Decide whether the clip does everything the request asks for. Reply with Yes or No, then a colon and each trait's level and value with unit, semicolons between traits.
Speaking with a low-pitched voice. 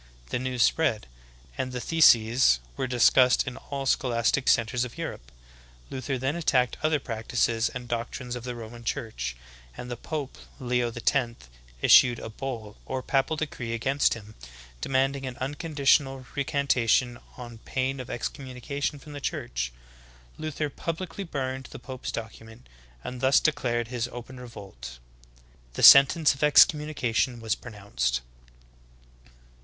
Yes: low, 125 Hz